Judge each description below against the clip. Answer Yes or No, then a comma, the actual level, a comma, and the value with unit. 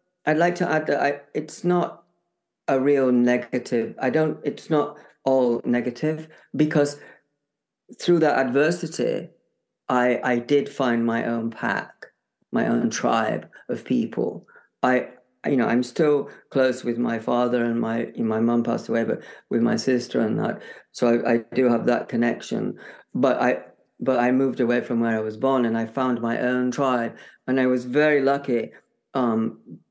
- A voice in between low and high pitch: No, low, 130 Hz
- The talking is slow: No, average, 170 wpm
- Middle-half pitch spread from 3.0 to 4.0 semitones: Yes, average, 3.3 semitones